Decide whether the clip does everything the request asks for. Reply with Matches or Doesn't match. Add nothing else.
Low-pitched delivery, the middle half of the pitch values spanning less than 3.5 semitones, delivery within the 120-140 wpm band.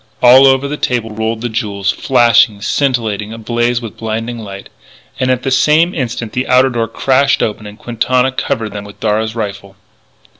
Doesn't match